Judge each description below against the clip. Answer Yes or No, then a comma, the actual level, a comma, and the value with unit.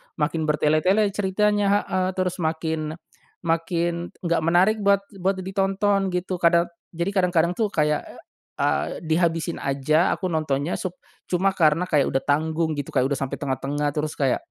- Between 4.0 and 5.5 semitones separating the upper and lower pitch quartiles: No, average, 3.5 semitones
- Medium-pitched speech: Yes, medium, 170 Hz